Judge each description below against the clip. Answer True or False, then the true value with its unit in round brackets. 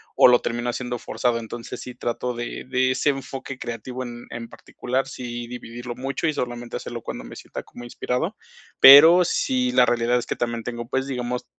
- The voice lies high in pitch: False (125 Hz)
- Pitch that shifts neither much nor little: False (1.9 semitones)